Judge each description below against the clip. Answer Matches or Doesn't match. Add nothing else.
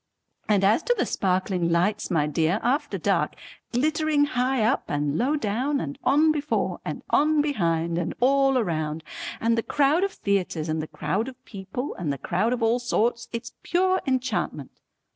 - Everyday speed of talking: Matches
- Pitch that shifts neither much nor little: Doesn't match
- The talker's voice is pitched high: Matches